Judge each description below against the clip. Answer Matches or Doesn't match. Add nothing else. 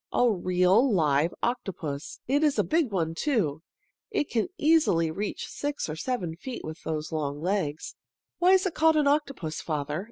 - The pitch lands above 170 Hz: Matches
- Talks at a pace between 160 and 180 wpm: Matches